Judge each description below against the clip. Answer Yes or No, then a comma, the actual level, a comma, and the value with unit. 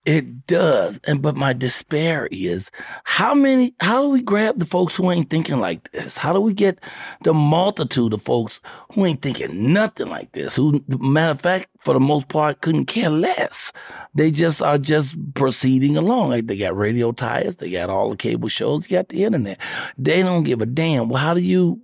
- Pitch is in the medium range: Yes, medium, 155 Hz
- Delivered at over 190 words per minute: Yes, fast, 205 wpm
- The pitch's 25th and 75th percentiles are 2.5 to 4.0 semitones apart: No, average, 5.0 semitones